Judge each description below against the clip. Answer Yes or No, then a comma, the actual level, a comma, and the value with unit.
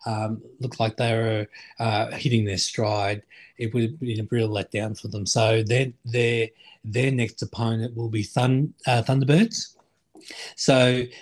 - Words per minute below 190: Yes, average, 160 wpm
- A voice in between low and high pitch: No, low, 115 Hz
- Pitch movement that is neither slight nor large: No, narrow, 2.3 semitones